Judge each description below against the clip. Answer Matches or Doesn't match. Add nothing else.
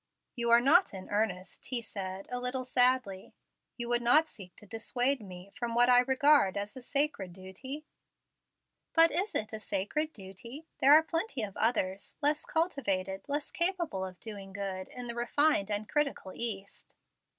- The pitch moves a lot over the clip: Matches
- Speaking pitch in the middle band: Doesn't match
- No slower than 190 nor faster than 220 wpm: Doesn't match